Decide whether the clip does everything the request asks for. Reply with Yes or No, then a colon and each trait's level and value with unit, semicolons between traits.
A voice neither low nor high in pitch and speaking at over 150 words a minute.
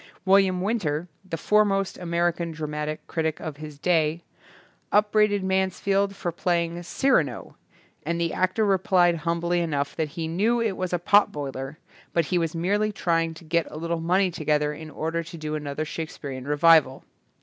Yes: medium, 170 Hz; average, 170 wpm